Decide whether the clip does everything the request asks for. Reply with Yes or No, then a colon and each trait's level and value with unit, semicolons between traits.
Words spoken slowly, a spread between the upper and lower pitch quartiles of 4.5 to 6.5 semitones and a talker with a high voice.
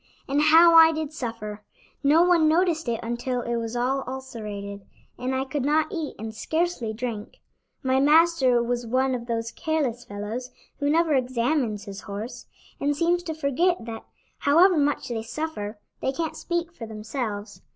No: average, 165 wpm; wide, 5.5 semitones; very high, 260 Hz